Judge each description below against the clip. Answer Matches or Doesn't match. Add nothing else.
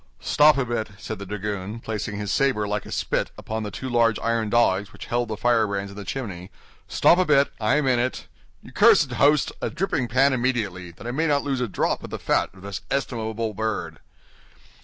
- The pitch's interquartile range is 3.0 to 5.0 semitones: Matches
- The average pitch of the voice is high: Doesn't match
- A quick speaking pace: Matches